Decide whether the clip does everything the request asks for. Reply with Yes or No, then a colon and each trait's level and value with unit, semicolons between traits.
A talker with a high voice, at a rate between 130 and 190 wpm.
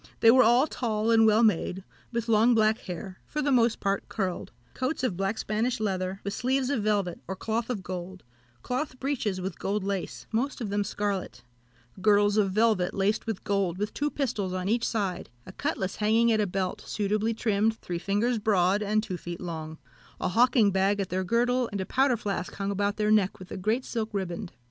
No: high, 210 Hz; fast, 205 wpm